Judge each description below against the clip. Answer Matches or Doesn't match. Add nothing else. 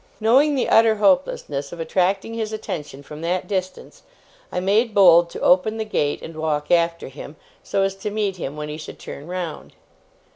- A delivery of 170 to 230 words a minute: Matches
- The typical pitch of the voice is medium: Matches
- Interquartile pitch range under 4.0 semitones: Doesn't match